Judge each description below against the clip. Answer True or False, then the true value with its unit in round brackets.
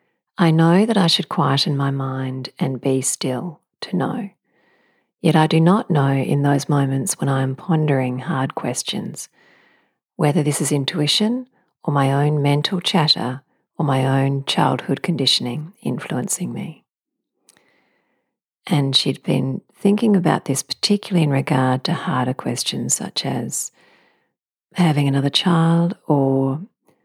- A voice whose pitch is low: False (145 Hz)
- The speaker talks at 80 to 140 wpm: True (135 wpm)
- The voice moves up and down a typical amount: True (4.0 semitones)